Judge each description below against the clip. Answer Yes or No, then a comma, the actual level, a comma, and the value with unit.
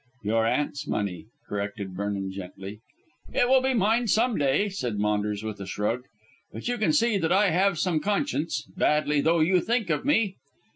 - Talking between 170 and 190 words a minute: Yes, average, 180 wpm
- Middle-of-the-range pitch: Yes, medium, 150 Hz